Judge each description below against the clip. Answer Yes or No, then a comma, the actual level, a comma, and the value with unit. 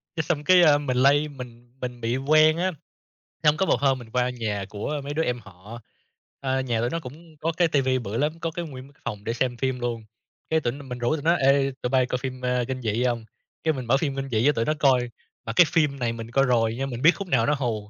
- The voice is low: Yes, low, 130 Hz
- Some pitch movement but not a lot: Yes, average, 3.6 semitones